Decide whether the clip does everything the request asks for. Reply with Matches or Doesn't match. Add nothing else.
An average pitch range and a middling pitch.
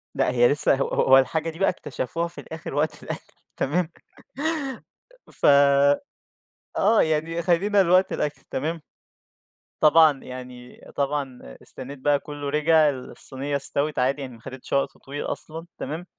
Matches